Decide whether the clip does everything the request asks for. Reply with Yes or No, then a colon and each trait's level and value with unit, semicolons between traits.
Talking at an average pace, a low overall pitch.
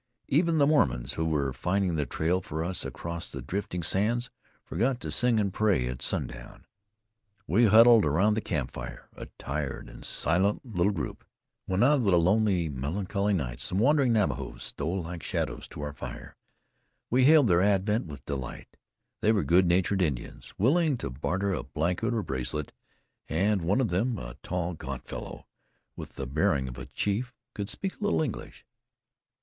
Yes: average, 175 wpm; very low, 95 Hz